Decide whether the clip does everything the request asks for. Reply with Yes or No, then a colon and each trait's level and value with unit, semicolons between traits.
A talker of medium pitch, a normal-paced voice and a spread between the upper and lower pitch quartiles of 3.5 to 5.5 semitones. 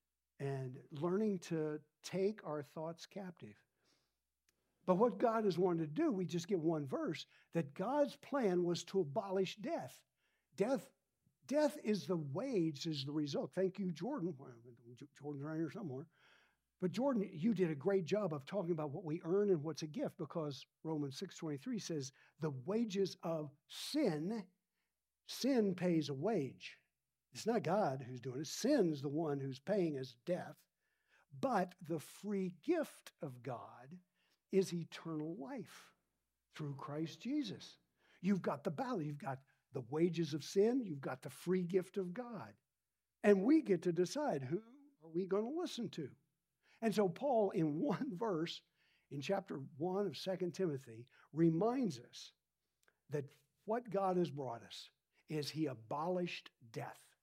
Yes: medium, 170 Hz; average, 155 wpm; average, 4.8 semitones